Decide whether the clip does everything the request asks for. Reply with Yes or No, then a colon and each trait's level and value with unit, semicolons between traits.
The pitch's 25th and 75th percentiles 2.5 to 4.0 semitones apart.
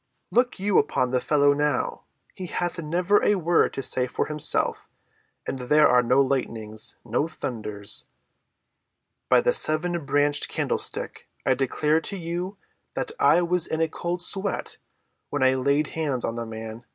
No: wide, 5.4 semitones